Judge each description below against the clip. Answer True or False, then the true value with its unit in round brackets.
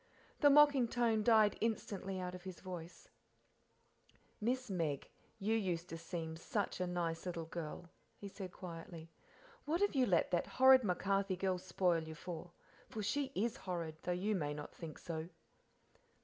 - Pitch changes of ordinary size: True (4.6 semitones)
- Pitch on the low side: False (185 Hz)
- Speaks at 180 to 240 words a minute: False (165 wpm)